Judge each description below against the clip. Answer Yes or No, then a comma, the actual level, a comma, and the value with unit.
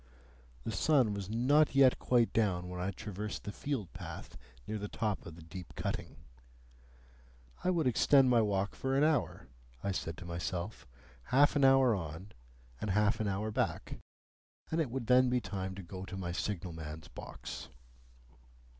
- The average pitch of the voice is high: No, low, 105 Hz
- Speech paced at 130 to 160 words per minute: No, average, 170 wpm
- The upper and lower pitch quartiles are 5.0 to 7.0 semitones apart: Yes, wide, 5.6 semitones